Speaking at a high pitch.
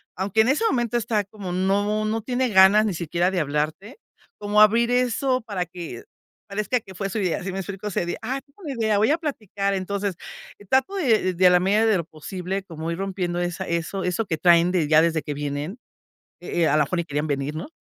Yes: high, 195 Hz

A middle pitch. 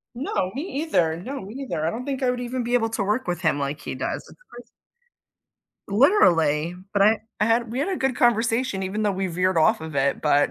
No: high, 210 Hz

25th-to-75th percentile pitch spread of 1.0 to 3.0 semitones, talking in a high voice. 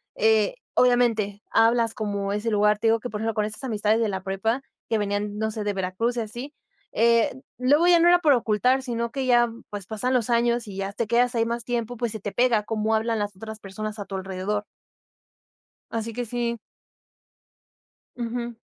Yes: narrow, 2.4 semitones; high, 225 Hz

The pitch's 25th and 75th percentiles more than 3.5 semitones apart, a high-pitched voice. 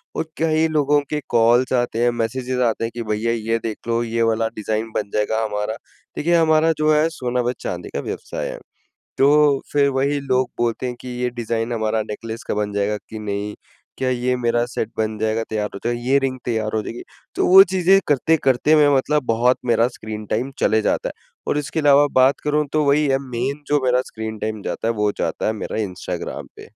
No: average, 4.2 semitones; low, 120 Hz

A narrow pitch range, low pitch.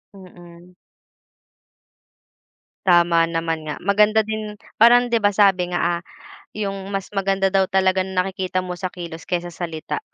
No: narrow, 2.2 semitones; medium, 185 Hz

